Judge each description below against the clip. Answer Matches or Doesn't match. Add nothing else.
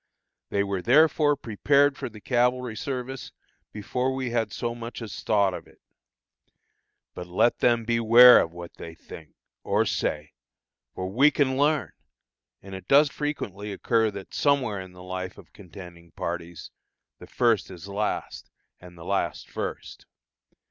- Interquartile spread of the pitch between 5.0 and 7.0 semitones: Matches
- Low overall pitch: Matches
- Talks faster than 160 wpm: Doesn't match